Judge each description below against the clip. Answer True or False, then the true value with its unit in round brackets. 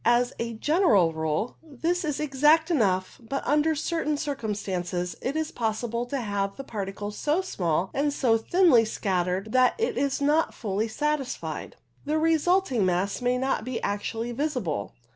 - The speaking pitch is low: False (245 Hz)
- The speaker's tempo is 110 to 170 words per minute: True (155 wpm)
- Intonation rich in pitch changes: True (6.7 semitones)